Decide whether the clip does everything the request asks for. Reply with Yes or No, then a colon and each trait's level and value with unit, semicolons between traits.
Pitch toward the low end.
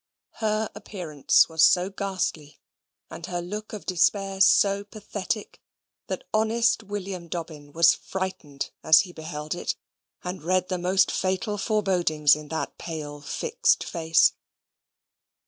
No: medium, 185 Hz